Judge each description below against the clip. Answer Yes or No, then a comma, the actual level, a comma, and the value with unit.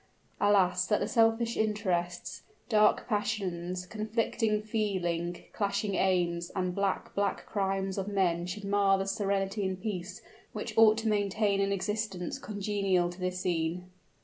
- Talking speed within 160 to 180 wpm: No, average, 140 wpm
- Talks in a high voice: Yes, high, 195 Hz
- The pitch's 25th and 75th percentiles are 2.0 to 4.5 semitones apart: Yes, narrow, 2.5 semitones